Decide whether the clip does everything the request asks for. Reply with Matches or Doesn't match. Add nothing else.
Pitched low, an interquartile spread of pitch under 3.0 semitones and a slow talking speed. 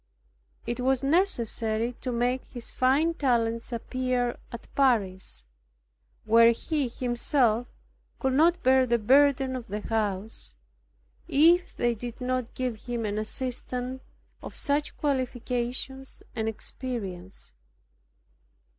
Doesn't match